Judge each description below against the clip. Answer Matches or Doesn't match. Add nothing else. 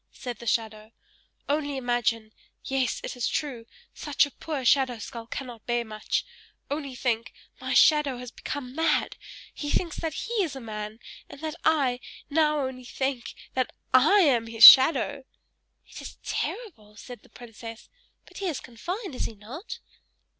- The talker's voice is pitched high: Matches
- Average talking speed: Matches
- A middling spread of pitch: Matches